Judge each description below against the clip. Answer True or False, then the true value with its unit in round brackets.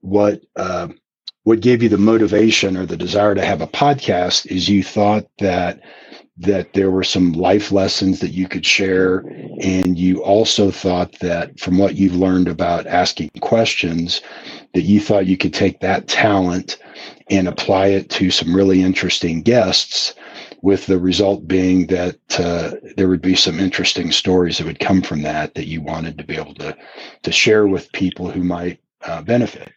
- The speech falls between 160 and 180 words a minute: True (175 wpm)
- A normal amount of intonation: False (1.8 semitones)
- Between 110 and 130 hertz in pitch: False (95 Hz)